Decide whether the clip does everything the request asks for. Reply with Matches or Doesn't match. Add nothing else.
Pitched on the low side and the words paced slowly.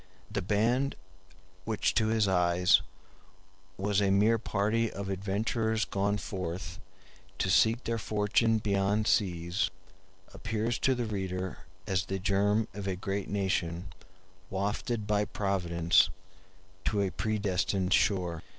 Matches